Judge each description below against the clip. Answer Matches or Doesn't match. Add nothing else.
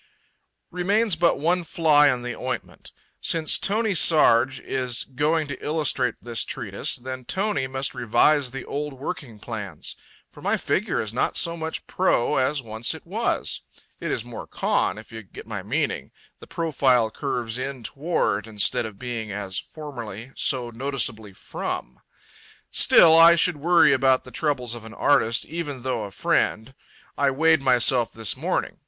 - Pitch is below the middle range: Matches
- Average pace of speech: Matches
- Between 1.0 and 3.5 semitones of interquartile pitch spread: Doesn't match